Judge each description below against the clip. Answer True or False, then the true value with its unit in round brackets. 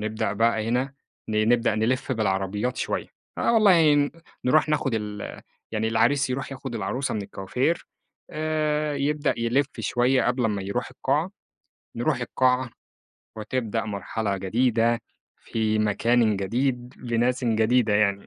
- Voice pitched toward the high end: False (120 Hz)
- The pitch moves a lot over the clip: False (3.6 semitones)